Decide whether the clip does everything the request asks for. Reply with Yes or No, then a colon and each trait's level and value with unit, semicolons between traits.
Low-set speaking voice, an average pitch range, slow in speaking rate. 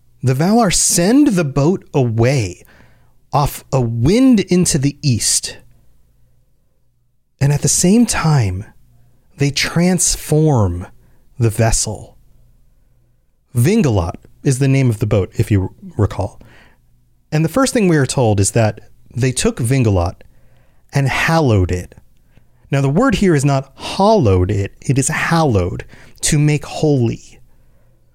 No: low, 130 Hz; wide, 6.6 semitones; slow, 130 wpm